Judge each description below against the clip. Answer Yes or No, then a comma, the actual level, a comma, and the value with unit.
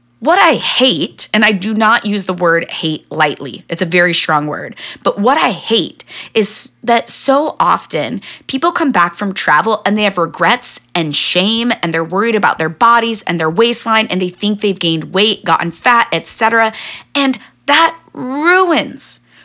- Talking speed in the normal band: Yes, average, 175 wpm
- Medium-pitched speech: No, high, 210 Hz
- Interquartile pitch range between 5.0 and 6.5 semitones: Yes, wide, 5.6 semitones